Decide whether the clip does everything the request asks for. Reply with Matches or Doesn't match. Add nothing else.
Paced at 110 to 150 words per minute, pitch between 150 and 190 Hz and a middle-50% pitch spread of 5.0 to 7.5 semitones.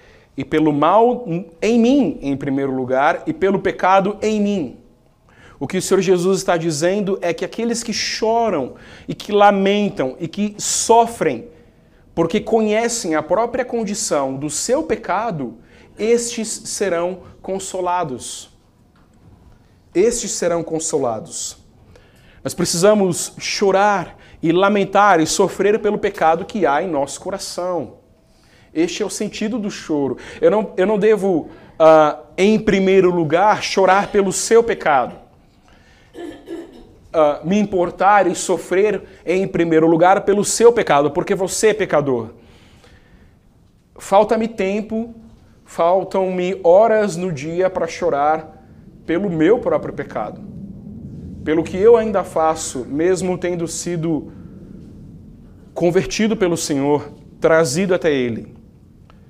Doesn't match